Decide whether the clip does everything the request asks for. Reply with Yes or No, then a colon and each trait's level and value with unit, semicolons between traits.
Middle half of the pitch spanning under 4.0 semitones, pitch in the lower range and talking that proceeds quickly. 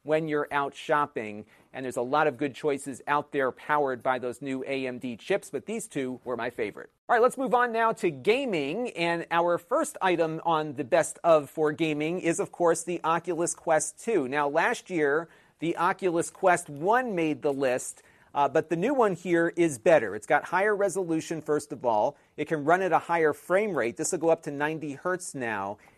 No: average, 3.3 semitones; medium, 160 Hz; fast, 210 wpm